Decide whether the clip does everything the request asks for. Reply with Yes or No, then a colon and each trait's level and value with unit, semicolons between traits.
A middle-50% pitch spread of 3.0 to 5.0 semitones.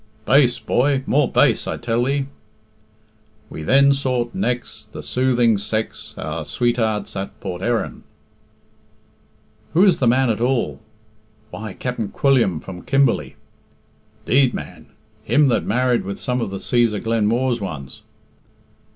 Yes: average, 3.3 semitones